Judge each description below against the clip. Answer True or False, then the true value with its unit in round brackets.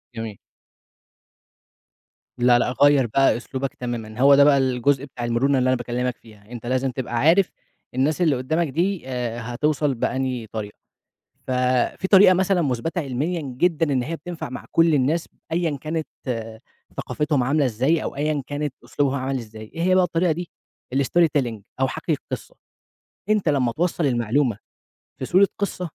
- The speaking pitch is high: False (135 Hz)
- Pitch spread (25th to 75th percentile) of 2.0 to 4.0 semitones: False (4.8 semitones)